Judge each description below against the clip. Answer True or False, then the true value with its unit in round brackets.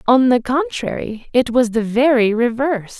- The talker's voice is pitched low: False (250 Hz)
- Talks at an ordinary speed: True (160 wpm)